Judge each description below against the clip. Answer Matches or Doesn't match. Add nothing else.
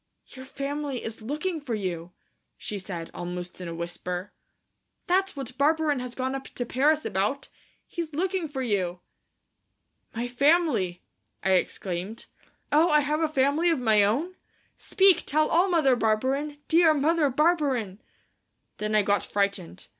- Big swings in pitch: Matches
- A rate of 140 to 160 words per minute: Matches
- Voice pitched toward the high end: Matches